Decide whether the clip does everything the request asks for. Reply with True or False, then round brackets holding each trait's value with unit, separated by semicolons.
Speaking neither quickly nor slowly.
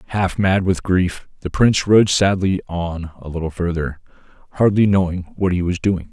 True (175 wpm)